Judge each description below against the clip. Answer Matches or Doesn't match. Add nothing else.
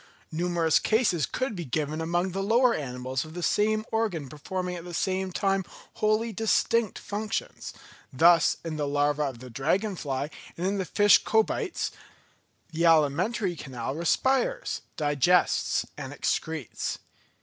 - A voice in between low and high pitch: Matches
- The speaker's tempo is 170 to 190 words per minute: Doesn't match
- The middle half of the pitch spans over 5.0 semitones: Matches